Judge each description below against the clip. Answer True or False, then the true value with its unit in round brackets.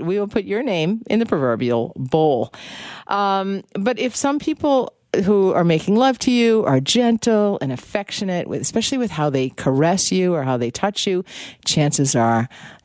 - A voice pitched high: True (195 Hz)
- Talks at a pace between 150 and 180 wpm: True (175 wpm)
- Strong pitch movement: True (7.3 semitones)